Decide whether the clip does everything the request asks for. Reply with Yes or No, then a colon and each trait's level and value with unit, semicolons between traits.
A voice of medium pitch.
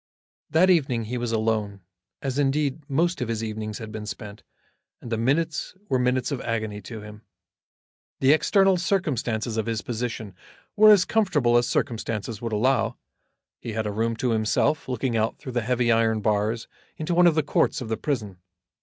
No: low, 120 Hz